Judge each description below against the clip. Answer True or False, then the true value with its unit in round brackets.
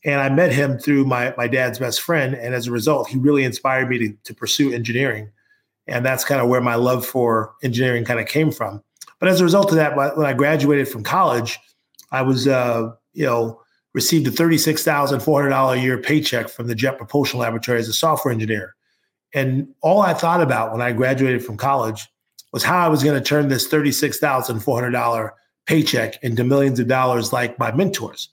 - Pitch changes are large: False (3.3 semitones)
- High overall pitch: False (130 Hz)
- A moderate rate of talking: False (220 wpm)